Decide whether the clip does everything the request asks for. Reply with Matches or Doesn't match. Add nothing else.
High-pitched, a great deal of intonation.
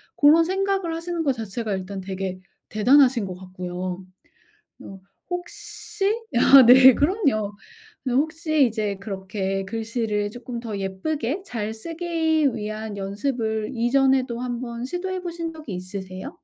Matches